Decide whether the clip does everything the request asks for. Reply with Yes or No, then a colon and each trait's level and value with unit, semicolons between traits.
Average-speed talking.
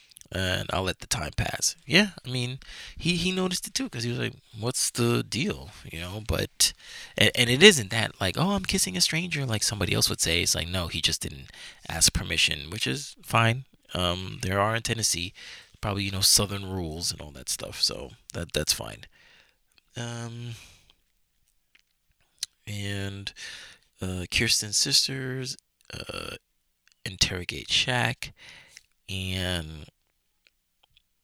Yes: average, 150 wpm